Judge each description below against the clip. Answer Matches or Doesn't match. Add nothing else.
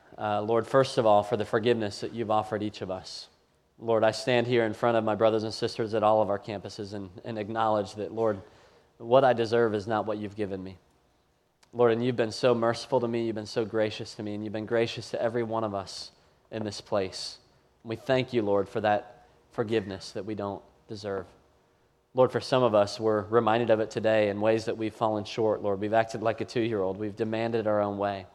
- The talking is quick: Matches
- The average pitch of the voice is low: Matches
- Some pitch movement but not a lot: Doesn't match